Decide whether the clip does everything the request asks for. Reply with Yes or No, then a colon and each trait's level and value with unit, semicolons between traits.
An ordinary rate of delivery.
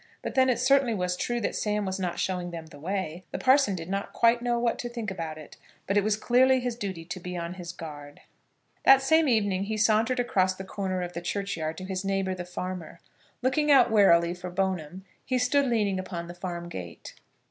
No: fast, 220 wpm